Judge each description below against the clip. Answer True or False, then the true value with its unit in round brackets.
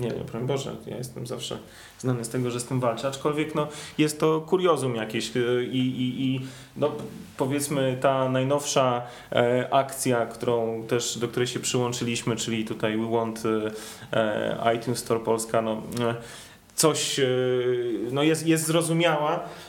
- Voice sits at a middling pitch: False (125 Hz)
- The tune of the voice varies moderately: True (3.4 semitones)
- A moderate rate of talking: True (145 wpm)